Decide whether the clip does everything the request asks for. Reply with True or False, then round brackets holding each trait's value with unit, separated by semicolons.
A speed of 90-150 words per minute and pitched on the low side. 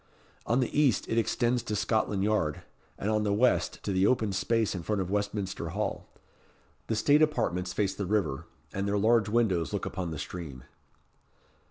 False (180 wpm; 105 Hz)